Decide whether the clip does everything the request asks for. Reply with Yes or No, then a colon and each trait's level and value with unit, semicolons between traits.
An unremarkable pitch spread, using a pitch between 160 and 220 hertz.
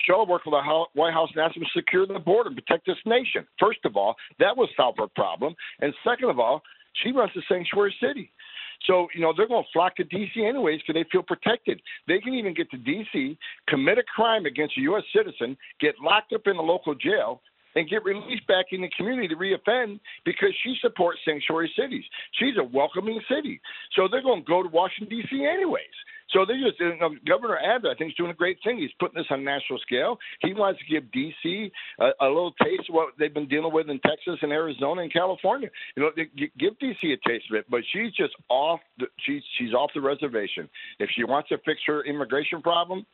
No: wide, 6.9 semitones; medium, 185 Hz